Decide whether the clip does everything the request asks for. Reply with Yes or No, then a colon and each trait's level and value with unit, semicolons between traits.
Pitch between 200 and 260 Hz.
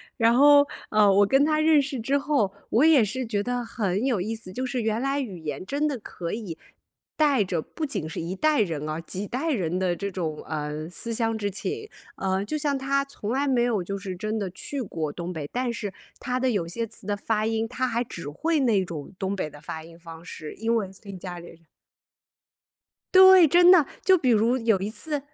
Yes: high, 220 Hz